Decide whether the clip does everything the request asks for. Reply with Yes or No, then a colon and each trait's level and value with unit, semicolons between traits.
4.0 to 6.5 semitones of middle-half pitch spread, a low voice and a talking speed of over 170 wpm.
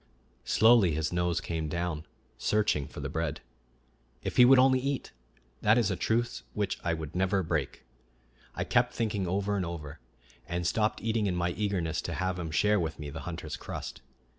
Yes: average, 4.6 semitones; very low, 90 Hz; average, 185 wpm